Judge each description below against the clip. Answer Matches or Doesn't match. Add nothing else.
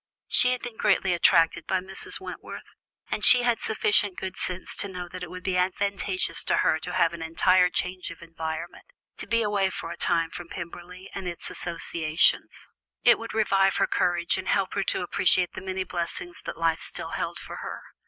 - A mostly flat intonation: Matches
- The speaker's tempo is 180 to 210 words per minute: Matches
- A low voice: Doesn't match